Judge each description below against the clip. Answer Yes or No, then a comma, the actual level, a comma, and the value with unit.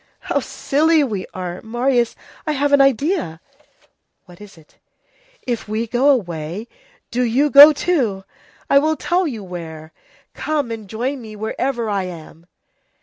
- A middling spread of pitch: No, wide, 6.6 semitones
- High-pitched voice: Yes, high, 235 Hz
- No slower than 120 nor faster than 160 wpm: Yes, average, 145 wpm